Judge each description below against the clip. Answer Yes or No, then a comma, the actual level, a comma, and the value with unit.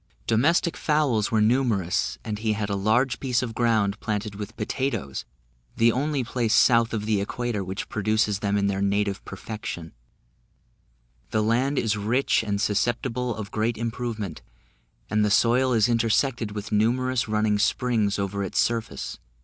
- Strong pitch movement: No, average, 2.8 semitones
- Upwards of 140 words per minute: Yes, average, 155 wpm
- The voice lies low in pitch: Yes, low, 110 Hz